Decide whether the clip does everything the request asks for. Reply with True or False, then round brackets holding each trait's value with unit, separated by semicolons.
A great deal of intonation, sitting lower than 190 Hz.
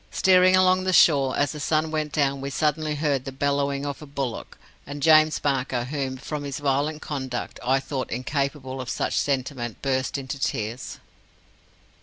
False (2.4 semitones; 140 Hz)